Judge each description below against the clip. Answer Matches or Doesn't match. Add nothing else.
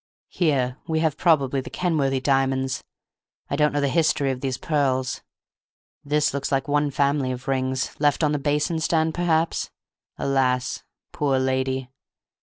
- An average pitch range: Doesn't match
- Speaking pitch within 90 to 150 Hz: Matches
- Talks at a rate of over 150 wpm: Doesn't match